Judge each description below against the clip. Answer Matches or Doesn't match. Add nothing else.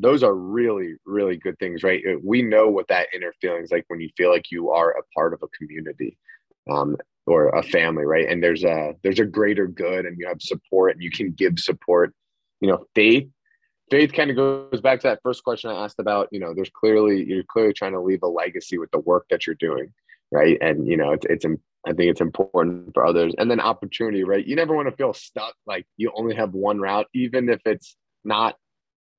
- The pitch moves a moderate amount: Doesn't match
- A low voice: Matches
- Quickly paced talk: Matches